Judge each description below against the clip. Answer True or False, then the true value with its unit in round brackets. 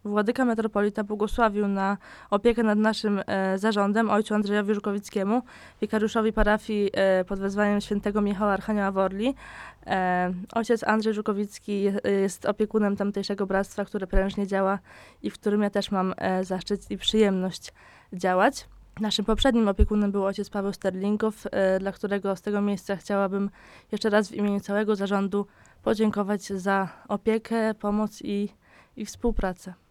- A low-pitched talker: False (205 Hz)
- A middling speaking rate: True (140 wpm)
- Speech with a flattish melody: True (1.5 semitones)